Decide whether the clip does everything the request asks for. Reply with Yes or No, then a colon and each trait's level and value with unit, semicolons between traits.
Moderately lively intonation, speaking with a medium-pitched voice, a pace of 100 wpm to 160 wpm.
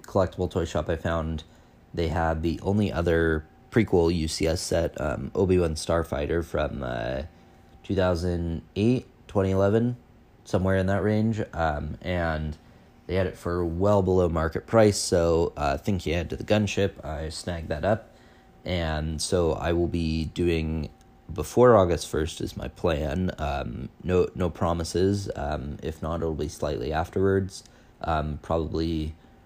No: average, 3.3 semitones; very low, 85 Hz; average, 145 wpm